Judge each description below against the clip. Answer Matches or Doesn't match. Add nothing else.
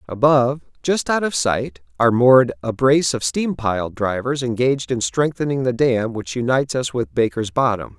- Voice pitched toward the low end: Matches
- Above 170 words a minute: Matches